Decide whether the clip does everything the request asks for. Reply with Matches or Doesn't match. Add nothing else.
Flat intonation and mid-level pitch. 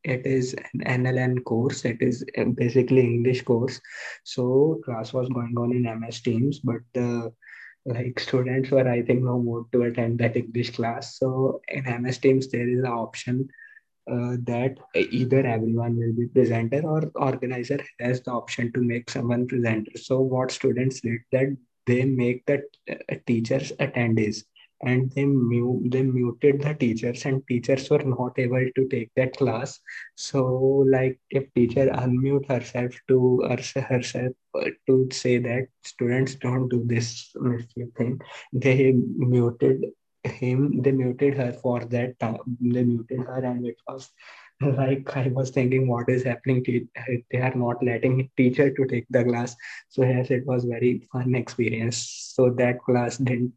Doesn't match